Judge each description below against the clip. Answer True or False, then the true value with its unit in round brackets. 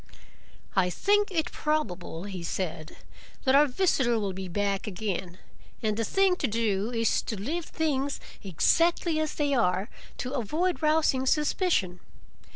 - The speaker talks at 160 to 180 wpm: False (145 wpm)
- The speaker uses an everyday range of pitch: False (8.1 semitones)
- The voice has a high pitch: True (240 Hz)